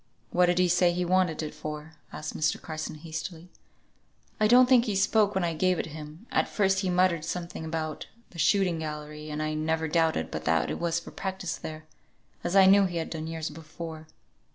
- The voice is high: No, medium, 165 Hz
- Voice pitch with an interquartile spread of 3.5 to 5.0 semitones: No, average, 2.9 semitones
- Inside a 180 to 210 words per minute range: Yes, fast, 205 wpm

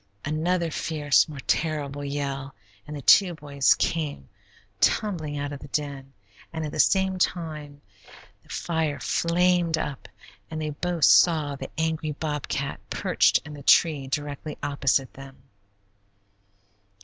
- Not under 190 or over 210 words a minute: No, slow, 135 wpm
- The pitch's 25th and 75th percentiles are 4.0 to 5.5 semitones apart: No, narrow, 2.4 semitones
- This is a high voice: No, medium, 150 Hz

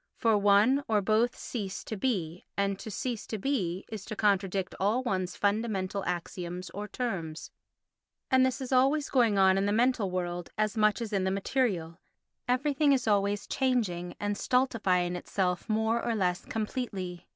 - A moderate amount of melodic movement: Yes, average, 4.3 semitones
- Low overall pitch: No, high, 205 Hz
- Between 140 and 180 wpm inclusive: Yes, average, 165 wpm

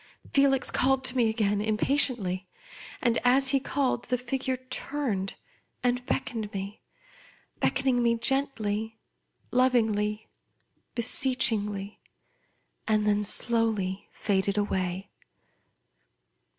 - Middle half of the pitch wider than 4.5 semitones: No, average, 3.8 semitones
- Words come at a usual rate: No, slow, 100 wpm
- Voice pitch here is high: Yes, high, 230 Hz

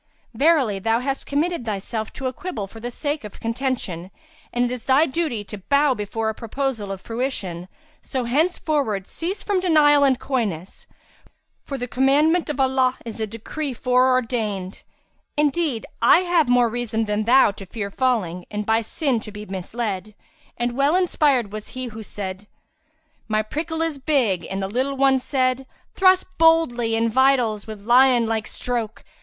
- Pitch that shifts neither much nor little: Yes, average, 4.4 semitones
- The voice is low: No, high, 245 Hz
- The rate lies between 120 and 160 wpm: No, average, 170 wpm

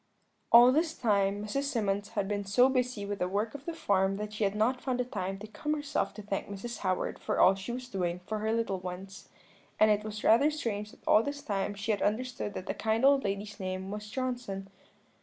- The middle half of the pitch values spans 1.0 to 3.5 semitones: No, average, 3.9 semitones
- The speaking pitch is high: Yes, high, 210 Hz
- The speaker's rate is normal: No, fast, 225 wpm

